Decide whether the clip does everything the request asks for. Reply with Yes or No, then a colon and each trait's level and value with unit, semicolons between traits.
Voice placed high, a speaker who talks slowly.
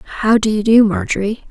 No: high, 220 Hz; average, 200 wpm